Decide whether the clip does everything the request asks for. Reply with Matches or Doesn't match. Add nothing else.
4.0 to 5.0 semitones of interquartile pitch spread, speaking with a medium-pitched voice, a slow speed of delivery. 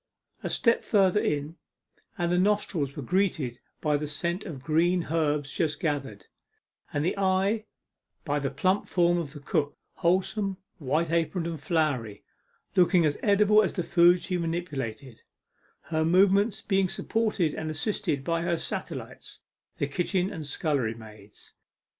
Doesn't match